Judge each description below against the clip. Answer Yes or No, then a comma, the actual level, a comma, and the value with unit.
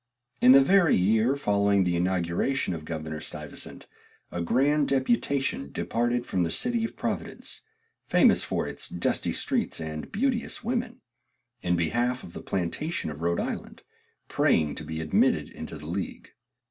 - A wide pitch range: Yes, wide, 9.0 semitones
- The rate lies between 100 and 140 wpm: No, average, 150 wpm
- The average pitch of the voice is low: Yes, low, 100 Hz